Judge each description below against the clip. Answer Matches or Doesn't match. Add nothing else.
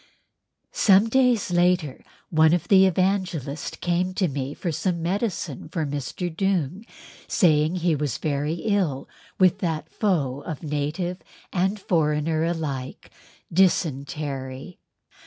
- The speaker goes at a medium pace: Doesn't match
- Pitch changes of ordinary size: Matches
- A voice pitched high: Doesn't match